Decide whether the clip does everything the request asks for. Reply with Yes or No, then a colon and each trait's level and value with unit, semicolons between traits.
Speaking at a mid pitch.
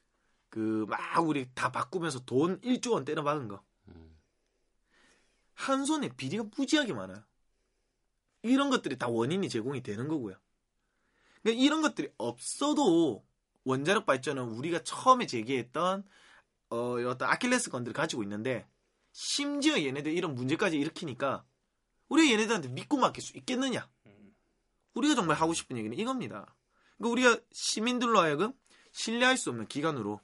Yes: medium, 175 Hz